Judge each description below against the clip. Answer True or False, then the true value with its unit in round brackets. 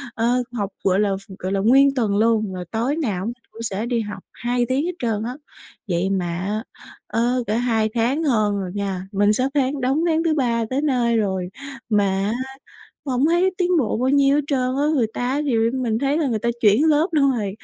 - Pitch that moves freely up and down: False (4.9 semitones)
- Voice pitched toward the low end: False (235 Hz)